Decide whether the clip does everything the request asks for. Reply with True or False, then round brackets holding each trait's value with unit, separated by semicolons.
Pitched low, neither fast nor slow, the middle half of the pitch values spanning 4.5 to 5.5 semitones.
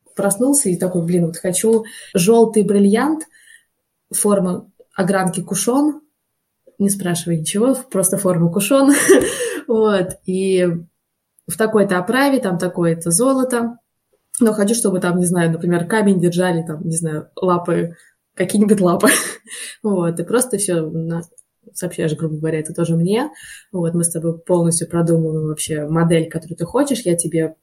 False (185 Hz; 140 wpm; 4.8 semitones)